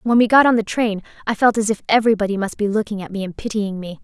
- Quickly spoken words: Yes, fast, 285 wpm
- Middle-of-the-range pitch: No, high, 210 Hz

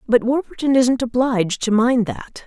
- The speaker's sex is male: No, female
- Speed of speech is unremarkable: Yes, average, 170 wpm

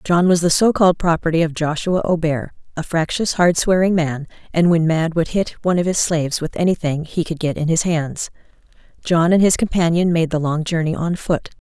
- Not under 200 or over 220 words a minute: Yes, fast, 205 wpm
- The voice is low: No, medium, 165 Hz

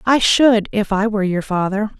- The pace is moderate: No, fast, 210 wpm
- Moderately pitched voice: No, high, 210 Hz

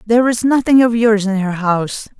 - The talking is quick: Yes, fast, 220 wpm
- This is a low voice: No, high, 220 Hz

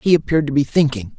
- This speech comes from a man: Yes, male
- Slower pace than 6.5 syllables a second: No, 7.0 syllables/s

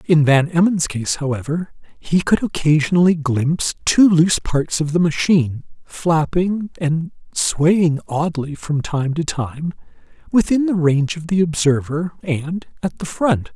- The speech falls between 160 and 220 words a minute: No, average, 145 wpm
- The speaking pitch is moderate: Yes, medium, 160 Hz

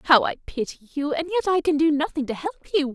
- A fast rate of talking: Yes, fast, 265 wpm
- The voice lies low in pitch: No, very high, 290 Hz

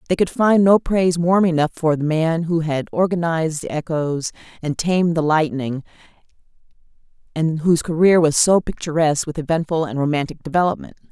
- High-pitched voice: No, medium, 160 Hz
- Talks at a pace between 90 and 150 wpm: No, average, 160 wpm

